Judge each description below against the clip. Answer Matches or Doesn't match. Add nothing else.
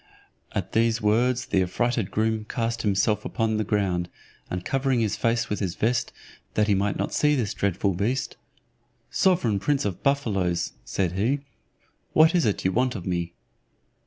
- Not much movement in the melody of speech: Doesn't match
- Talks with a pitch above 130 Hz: Doesn't match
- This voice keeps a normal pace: Matches